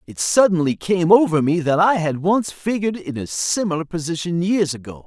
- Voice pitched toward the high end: No, medium, 170 Hz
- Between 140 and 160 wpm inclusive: No, average, 190 wpm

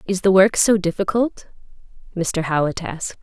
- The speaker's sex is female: Yes, female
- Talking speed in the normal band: Yes, average, 150 wpm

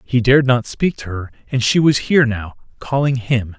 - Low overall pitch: Yes, low, 125 Hz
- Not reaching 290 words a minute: Yes, average, 200 wpm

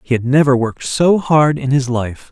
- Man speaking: Yes, male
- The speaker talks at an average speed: No, fast, 235 wpm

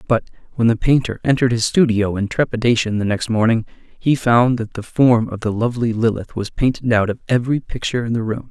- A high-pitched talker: No, low, 115 Hz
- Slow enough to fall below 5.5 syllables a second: No, 5.9 syllables/s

